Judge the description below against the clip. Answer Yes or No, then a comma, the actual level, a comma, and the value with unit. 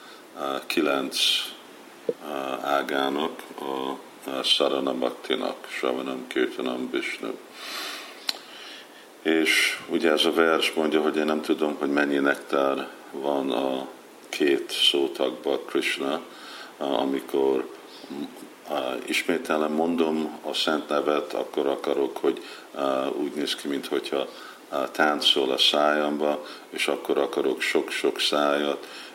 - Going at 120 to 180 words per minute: No, average, 110 wpm